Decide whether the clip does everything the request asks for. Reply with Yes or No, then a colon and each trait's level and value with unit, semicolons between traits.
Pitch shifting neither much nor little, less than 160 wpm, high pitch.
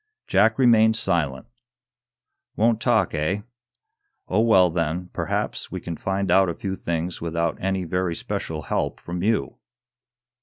No: average, 3.6 semitones; average, 140 wpm; very low, 90 Hz